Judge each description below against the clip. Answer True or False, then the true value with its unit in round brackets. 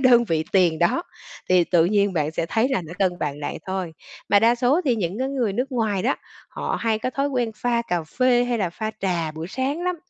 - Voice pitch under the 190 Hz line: False (215 Hz)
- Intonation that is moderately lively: False (6.1 semitones)